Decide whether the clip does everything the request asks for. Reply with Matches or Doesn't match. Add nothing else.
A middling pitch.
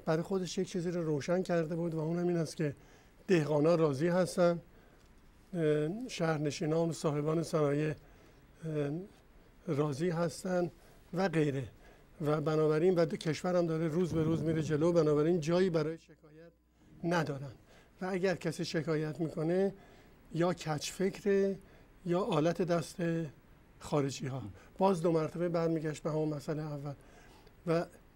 Matches